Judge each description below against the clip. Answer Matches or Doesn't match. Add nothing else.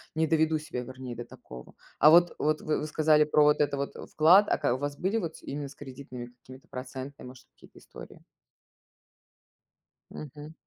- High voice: Doesn't match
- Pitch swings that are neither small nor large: Matches